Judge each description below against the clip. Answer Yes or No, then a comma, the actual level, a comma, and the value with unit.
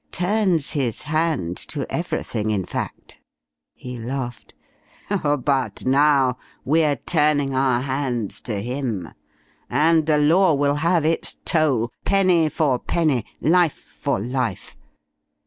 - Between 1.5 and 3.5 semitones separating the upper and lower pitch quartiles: No, average, 4.2 semitones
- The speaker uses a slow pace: Yes, slow, 115 wpm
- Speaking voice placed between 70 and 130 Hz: No, medium, 140 Hz